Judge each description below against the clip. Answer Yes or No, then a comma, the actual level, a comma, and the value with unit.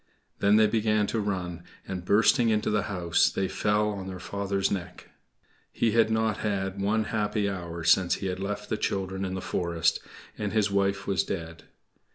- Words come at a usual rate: Yes, average, 185 wpm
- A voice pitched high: No, low, 100 Hz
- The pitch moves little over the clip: Yes, narrow, 2.0 semitones